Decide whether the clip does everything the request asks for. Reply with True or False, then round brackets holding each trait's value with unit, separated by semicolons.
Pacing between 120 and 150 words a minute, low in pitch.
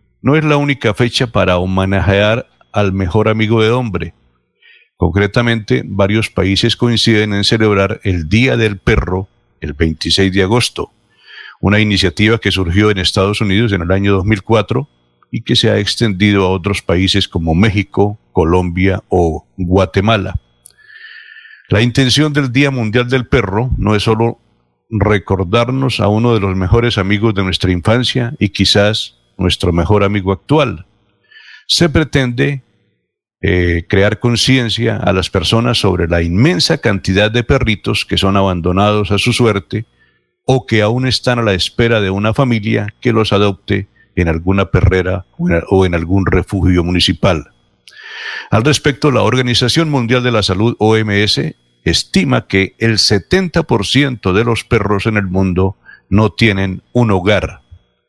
True (145 wpm; 105 Hz)